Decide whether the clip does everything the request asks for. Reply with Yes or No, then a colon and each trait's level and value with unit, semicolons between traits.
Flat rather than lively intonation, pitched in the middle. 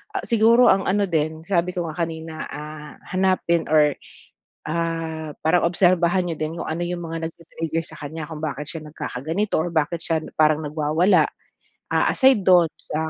Yes: narrow, 2.2 semitones; medium, 165 Hz